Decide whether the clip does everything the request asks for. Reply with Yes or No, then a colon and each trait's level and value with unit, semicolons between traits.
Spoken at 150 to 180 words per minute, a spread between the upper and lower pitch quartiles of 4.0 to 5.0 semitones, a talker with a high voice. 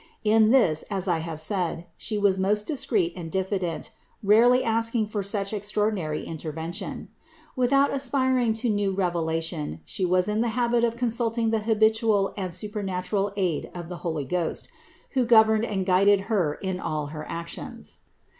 Yes: average, 160 wpm; average, 4.3 semitones; high, 205 Hz